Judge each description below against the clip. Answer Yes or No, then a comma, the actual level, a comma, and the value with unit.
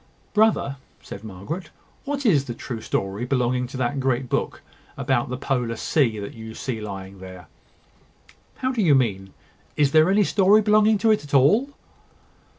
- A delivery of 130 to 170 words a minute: Yes, average, 165 wpm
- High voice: No, low, 135 Hz